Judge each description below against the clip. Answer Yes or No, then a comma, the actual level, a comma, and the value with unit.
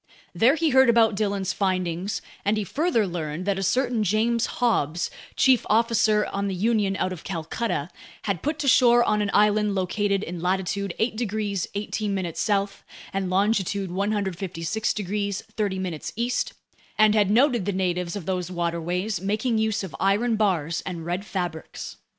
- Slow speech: No, average, 160 wpm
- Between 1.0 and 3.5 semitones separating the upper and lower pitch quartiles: Yes, average, 3.0 semitones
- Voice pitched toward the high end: Yes, high, 200 Hz